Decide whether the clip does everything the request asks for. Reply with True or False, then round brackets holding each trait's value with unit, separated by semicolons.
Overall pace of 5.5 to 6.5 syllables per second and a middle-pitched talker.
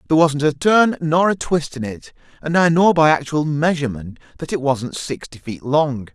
False (5.0 syllables/s; 150 Hz)